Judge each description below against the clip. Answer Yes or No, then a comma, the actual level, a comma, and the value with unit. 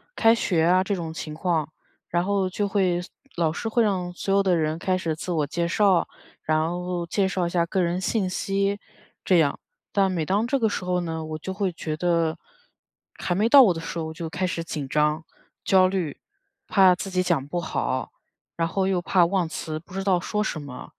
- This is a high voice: No, medium, 180 Hz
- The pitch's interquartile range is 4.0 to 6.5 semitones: No, average, 2.9 semitones